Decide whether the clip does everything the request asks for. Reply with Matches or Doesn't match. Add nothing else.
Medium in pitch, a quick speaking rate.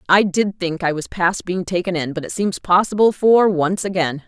Matches